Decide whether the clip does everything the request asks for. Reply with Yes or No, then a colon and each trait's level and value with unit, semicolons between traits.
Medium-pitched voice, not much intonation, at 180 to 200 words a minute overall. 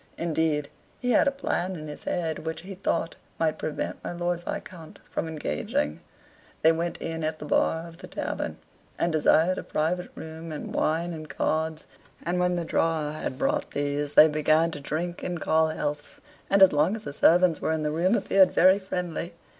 Yes: medium, 160 Hz; narrow, 2.3 semitones; average, 195 wpm